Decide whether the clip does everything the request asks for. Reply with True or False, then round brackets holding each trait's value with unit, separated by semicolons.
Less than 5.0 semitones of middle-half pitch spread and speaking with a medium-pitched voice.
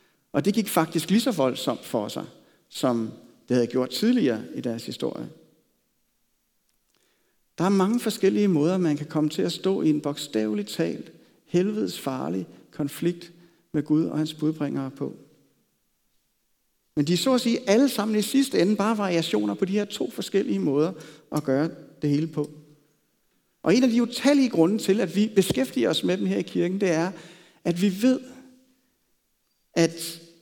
False (5.6 semitones; 170 Hz)